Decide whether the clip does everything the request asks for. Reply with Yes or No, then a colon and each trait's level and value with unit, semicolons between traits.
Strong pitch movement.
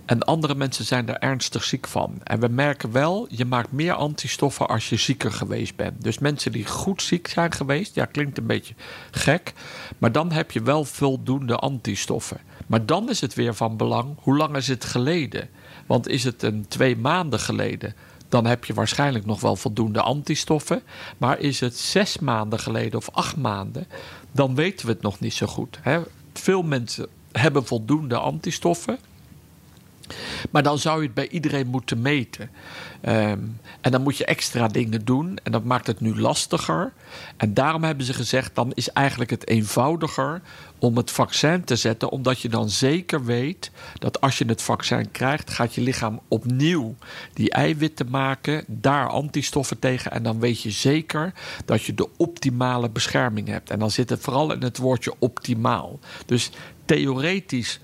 No: average, 3.8 semitones